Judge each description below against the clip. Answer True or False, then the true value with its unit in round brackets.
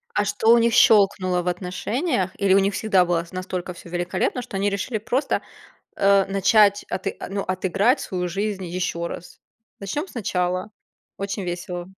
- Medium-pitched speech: False (195 Hz)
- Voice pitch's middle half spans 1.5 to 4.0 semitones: True (2.4 semitones)